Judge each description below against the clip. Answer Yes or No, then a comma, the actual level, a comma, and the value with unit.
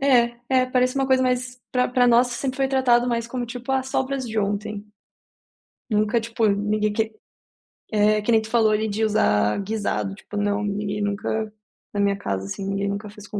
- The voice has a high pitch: Yes, high, 220 Hz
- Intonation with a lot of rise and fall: No, average, 3.3 semitones